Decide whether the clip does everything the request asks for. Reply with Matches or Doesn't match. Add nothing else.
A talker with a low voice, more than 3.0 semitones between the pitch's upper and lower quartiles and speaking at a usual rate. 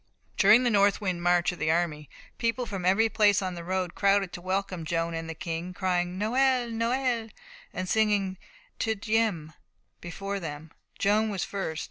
Doesn't match